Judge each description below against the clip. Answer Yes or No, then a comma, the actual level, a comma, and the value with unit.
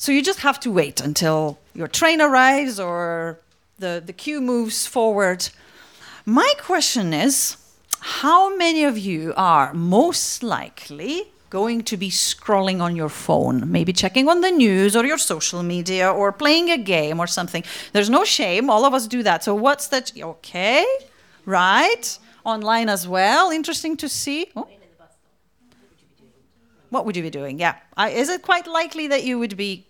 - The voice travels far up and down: Yes, wide, 8.4 semitones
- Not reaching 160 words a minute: No, average, 165 wpm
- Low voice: No, high, 225 Hz